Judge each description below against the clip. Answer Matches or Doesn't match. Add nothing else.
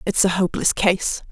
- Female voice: Matches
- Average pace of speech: Matches